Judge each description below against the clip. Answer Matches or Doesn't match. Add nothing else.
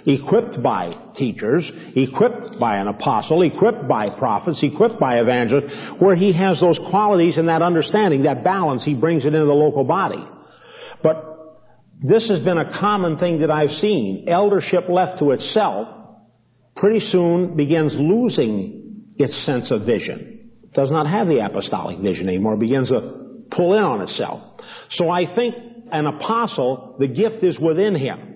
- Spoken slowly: Doesn't match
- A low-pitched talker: Doesn't match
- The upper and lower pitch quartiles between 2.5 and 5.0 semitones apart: Doesn't match